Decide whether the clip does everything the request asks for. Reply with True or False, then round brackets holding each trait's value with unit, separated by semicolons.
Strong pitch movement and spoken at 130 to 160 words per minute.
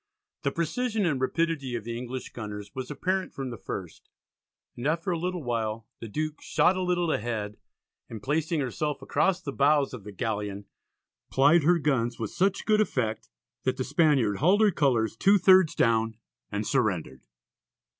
False (7.0 semitones; 170 wpm)